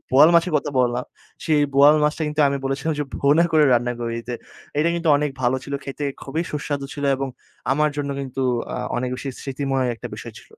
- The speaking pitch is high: No, medium, 140 Hz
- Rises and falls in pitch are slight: Yes, narrow, 2.3 semitones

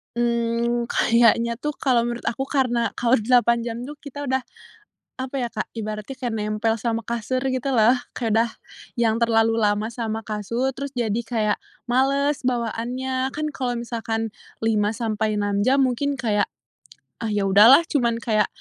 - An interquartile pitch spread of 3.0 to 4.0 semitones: No, narrow, 2.4 semitones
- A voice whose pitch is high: Yes, high, 235 Hz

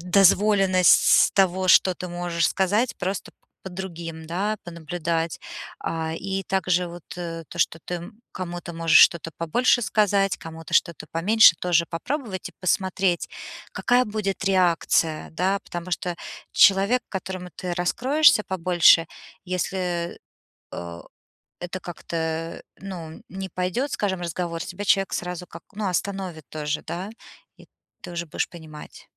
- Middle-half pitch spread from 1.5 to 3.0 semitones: Yes, narrow, 2.5 semitones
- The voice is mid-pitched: Yes, medium, 180 Hz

